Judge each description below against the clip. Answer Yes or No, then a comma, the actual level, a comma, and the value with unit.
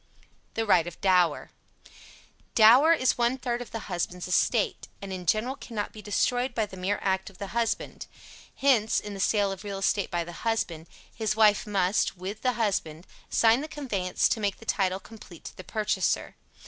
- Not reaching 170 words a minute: No, average, 185 wpm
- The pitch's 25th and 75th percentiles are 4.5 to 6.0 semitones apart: No, average, 3.5 semitones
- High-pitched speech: Yes, high, 205 Hz